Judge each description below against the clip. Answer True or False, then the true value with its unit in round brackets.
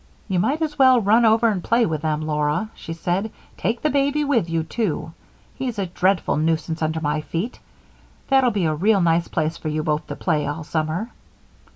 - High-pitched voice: False (175 Hz)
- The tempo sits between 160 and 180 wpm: False (200 wpm)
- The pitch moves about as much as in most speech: False (6.5 semitones)